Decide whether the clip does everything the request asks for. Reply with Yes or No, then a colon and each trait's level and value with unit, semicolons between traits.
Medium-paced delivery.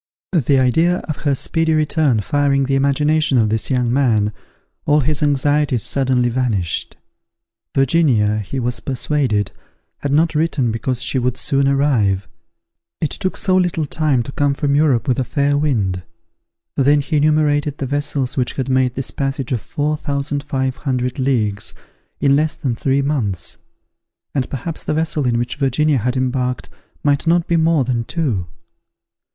Yes: average, 160 wpm